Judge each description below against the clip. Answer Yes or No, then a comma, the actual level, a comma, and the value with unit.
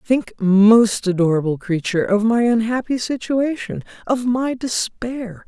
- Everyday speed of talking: No, slow, 120 wpm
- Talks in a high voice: Yes, high, 225 Hz